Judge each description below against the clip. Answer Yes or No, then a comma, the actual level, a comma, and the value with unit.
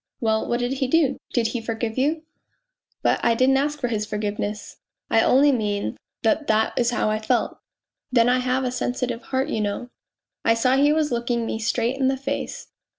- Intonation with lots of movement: No, average, 3.1 semitones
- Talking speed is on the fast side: Yes, fast, 210 wpm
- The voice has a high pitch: Yes, high, 245 Hz